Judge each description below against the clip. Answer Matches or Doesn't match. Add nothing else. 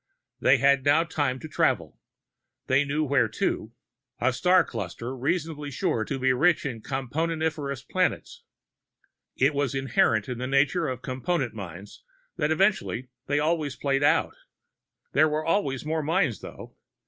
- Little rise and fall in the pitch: Doesn't match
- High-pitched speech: Doesn't match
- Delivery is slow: Doesn't match